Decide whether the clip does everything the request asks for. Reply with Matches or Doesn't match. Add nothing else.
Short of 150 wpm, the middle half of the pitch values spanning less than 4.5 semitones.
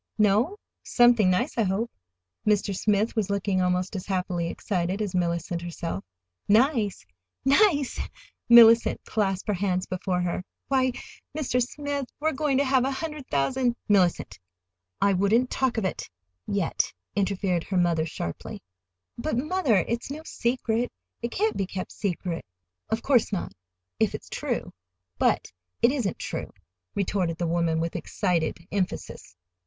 Doesn't match